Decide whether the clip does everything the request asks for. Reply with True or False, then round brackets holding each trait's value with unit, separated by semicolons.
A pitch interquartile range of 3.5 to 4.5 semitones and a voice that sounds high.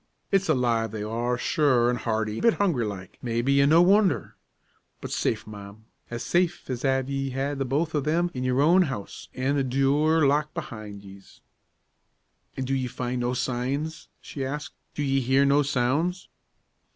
False (3.8 semitones; 135 Hz)